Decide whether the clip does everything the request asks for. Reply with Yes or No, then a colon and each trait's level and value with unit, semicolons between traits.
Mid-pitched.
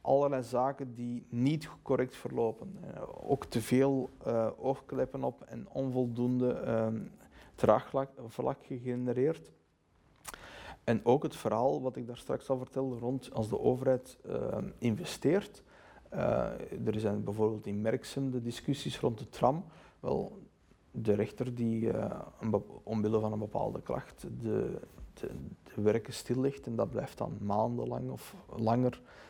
No: low, 120 Hz